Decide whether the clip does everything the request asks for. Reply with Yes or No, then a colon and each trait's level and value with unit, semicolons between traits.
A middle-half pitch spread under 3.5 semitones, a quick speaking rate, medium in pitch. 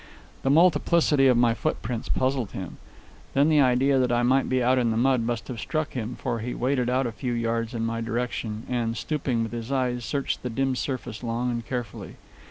No: narrow, 2.4 semitones; fast, 210 wpm; low, 125 Hz